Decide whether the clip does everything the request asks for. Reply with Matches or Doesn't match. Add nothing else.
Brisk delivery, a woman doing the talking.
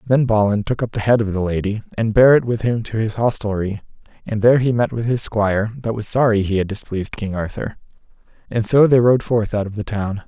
Doesn't match